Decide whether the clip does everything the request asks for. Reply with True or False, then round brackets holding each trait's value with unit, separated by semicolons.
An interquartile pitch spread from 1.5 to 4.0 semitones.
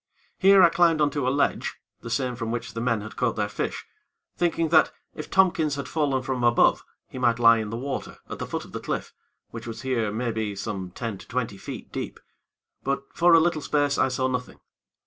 False (4.5 semitones)